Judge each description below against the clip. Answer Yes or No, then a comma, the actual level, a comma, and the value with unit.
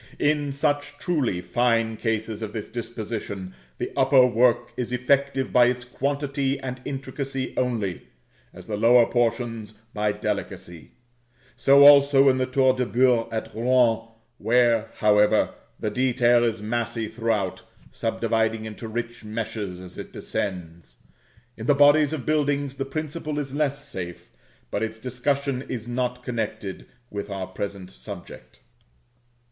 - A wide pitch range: No, average, 3.7 semitones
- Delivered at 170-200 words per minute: No, average, 140 wpm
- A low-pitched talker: Yes, low, 120 Hz